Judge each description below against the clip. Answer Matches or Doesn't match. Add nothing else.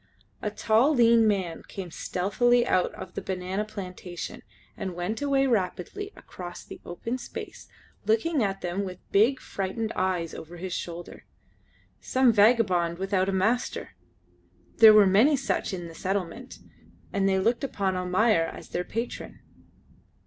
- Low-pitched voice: Doesn't match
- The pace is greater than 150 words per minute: Doesn't match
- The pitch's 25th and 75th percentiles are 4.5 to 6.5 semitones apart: Doesn't match